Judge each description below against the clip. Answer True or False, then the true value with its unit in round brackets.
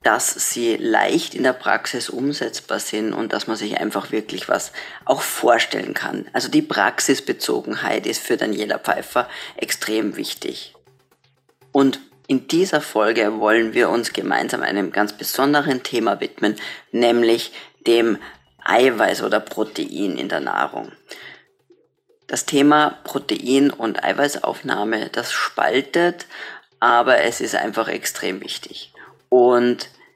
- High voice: False (135 Hz)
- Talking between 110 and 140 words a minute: True (125 wpm)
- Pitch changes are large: True (6.5 semitones)